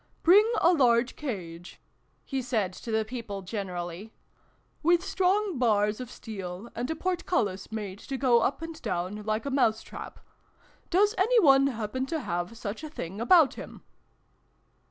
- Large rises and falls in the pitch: Yes, wide, 7.1 semitones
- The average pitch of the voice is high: Yes, high, 235 Hz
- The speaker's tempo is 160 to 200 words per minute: Yes, average, 165 wpm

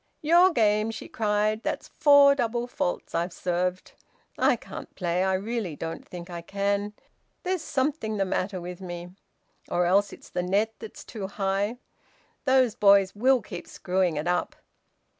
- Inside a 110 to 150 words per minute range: No, average, 160 wpm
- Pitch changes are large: No, average, 4.2 semitones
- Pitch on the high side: Yes, high, 200 Hz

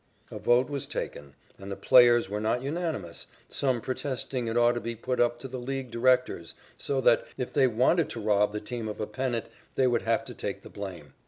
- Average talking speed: No, fast, 220 wpm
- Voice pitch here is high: No, low, 120 Hz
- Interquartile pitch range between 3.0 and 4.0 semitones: Yes, average, 3.3 semitones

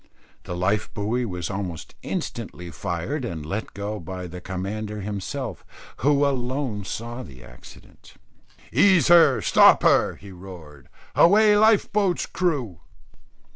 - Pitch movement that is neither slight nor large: No, wide, 7.6 semitones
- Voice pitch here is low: Yes, low, 105 Hz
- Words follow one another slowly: Yes, slow, 130 wpm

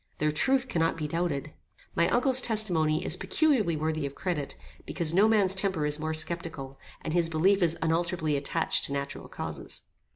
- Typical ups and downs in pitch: Yes, average, 3.7 semitones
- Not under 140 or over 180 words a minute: Yes, average, 170 wpm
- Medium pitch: Yes, medium, 165 Hz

